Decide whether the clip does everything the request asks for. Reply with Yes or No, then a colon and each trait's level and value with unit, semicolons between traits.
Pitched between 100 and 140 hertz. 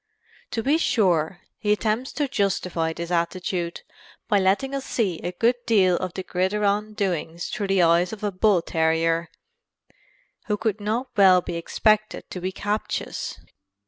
No: high, 195 Hz